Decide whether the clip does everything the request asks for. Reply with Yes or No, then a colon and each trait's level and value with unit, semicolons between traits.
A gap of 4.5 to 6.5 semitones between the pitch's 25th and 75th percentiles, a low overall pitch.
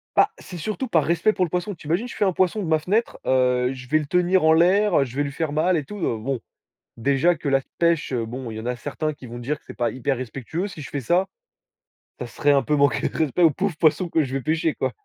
No: average, 4.8 semitones; medium, 155 Hz